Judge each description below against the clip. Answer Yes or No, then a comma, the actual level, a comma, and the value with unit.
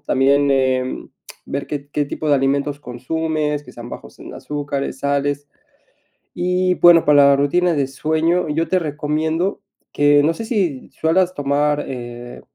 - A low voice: No, medium, 145 Hz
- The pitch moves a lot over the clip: No, narrow, 2.5 semitones